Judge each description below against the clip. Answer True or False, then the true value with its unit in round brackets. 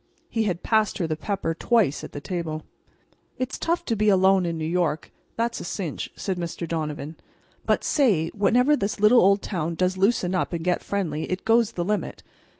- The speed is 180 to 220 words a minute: True (185 wpm)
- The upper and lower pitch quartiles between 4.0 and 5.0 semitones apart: True (4.4 semitones)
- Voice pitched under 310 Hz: True (185 Hz)